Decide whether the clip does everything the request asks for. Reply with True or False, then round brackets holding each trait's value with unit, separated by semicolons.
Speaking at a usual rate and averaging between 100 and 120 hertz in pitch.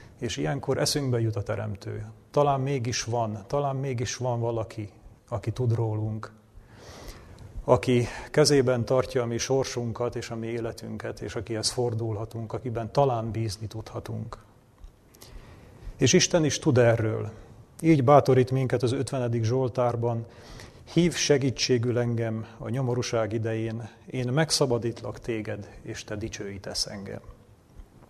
True (120 wpm; 115 Hz)